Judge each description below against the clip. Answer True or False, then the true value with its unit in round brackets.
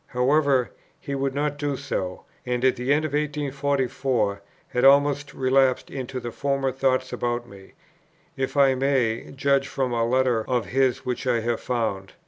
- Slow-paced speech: False (165 wpm)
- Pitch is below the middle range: True (130 Hz)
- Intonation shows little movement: True (2.3 semitones)